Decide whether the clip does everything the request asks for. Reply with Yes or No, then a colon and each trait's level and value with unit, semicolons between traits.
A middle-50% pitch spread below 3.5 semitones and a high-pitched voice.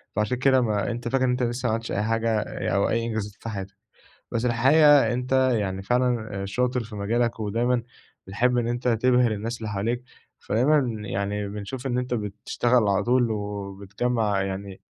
No: average, 3.1 semitones; low, 115 Hz